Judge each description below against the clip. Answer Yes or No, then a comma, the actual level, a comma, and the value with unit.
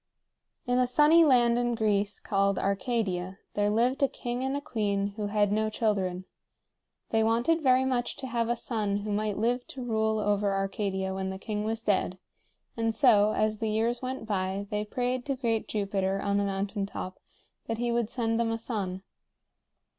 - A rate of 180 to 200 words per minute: Yes, average, 185 wpm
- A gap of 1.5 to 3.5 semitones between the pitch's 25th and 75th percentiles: Yes, average, 3.1 semitones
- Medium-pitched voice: No, high, 215 Hz